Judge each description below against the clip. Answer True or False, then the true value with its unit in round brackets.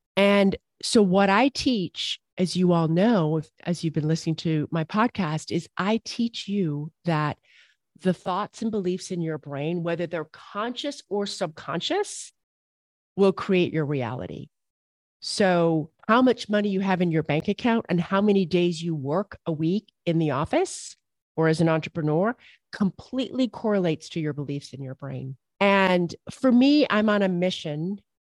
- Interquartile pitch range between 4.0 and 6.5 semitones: True (4.5 semitones)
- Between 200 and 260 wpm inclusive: False (165 wpm)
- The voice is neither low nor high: True (180 Hz)